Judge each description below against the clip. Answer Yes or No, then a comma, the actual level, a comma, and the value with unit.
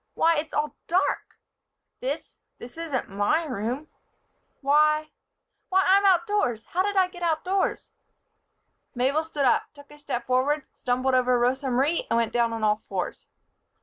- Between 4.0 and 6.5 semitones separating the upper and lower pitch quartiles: Yes, average, 5.0 semitones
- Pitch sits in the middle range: No, very high, 290 Hz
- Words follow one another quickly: No, average, 150 wpm